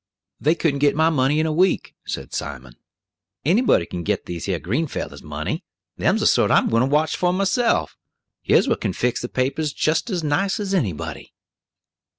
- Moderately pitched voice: Yes, medium, 150 Hz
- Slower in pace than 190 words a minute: No, average, 195 wpm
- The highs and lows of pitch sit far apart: Yes, wide, 6.9 semitones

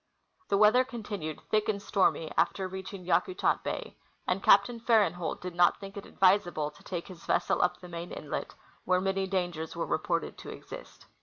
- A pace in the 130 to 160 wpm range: No, average, 180 wpm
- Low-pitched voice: No, high, 190 Hz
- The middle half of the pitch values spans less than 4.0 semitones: Yes, narrow, 2.4 semitones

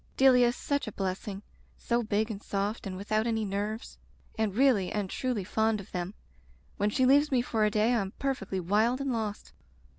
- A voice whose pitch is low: No, high, 215 Hz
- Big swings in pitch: No, average, 3.3 semitones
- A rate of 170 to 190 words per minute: No, average, 200 wpm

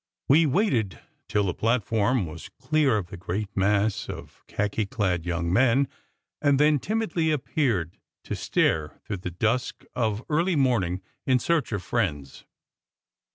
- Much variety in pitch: Yes, wide, 6.7 semitones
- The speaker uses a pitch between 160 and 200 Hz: No, low, 110 Hz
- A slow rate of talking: No, average, 150 wpm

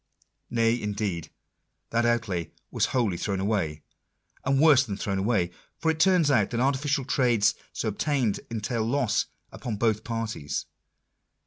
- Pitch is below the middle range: Yes, low, 115 Hz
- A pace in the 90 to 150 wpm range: Yes, average, 140 wpm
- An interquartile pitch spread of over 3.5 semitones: Yes, average, 4.3 semitones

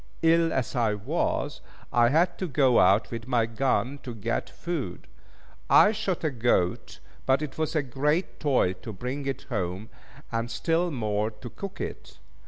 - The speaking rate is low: No, average, 170 wpm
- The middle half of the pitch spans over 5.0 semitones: Yes, wide, 5.5 semitones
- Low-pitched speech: Yes, low, 125 Hz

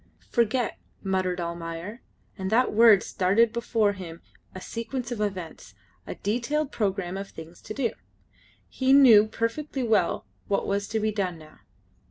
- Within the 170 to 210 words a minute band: No, average, 150 wpm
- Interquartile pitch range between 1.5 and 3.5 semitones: No, average, 4.0 semitones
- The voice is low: No, high, 210 Hz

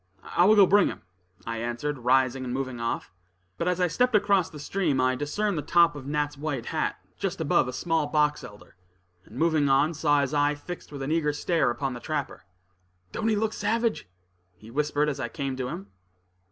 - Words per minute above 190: Yes, fast, 205 wpm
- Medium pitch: Yes, medium, 145 Hz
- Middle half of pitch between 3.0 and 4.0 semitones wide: No, average, 4.5 semitones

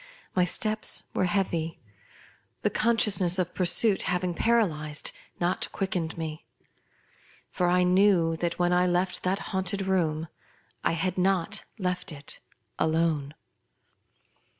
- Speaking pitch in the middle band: Yes, medium, 180 Hz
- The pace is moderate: No, slow, 120 wpm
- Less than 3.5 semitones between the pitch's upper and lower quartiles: Yes, narrow, 2.4 semitones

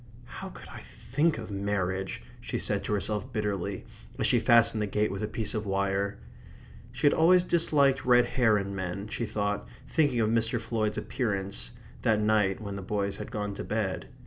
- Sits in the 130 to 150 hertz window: No, low, 105 Hz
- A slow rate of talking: No, average, 190 wpm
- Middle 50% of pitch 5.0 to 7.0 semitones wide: No, average, 3.1 semitones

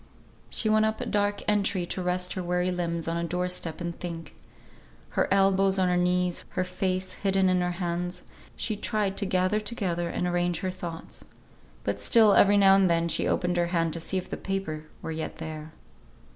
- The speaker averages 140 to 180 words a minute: No, average, 200 wpm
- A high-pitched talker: No, medium, 180 Hz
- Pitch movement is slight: Yes, narrow, 2.1 semitones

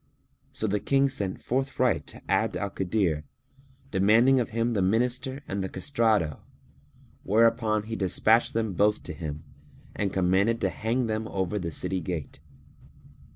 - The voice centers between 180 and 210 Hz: No, low, 105 Hz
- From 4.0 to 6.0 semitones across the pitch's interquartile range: No, average, 3.5 semitones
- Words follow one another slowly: No, average, 155 wpm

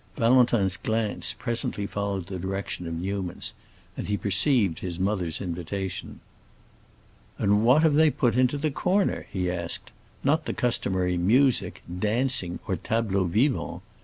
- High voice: No, low, 100 Hz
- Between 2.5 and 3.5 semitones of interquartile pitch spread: No, average, 5.2 semitones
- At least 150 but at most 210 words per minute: No, slow, 135 wpm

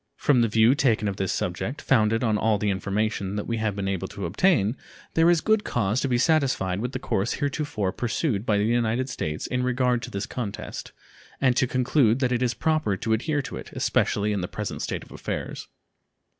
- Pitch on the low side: Yes, low, 115 Hz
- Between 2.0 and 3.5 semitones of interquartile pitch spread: No, average, 4.1 semitones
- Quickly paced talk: Yes, fast, 210 wpm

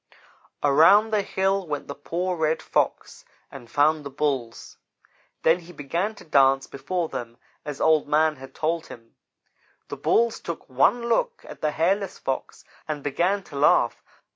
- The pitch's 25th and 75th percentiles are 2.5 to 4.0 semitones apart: No, average, 4.6 semitones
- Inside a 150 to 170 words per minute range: Yes, average, 160 wpm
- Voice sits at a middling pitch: Yes, medium, 155 Hz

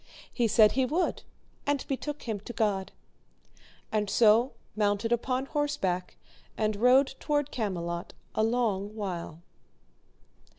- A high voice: Yes, high, 220 Hz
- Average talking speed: No, slow, 120 wpm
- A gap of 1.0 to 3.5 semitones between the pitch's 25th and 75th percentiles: No, average, 4.3 semitones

